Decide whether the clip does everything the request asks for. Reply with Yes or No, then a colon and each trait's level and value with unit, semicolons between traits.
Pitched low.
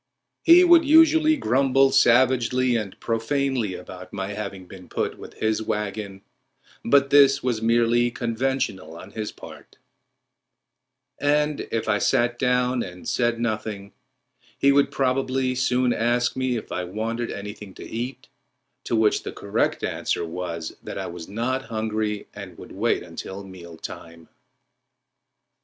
Yes: low, 115 Hz